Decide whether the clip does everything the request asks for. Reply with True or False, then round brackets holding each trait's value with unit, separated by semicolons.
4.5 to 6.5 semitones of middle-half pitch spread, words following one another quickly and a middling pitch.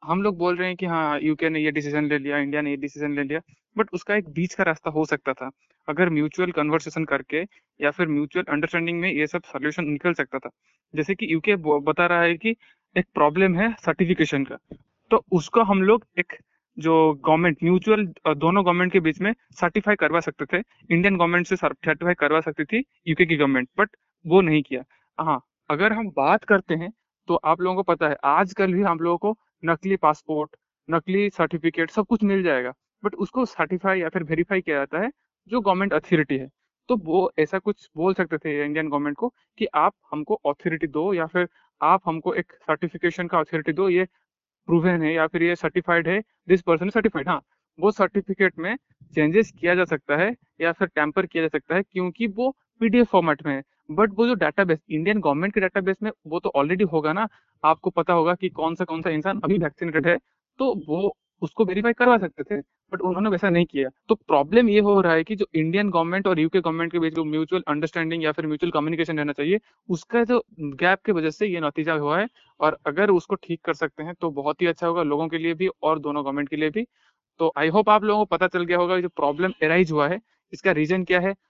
False (3.7 semitones; 220 wpm; 170 Hz)